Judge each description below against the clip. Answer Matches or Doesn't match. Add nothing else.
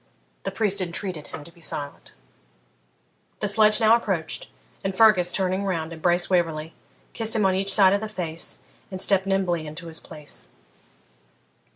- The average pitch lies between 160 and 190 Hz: Matches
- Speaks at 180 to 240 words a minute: Doesn't match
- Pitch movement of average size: Matches